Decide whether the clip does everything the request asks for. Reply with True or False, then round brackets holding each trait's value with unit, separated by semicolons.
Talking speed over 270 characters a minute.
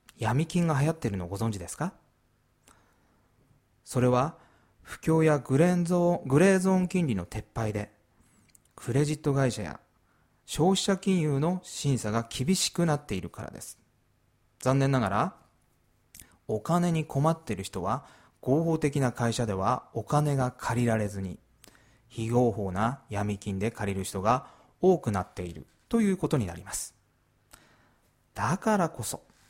False (265 characters per minute)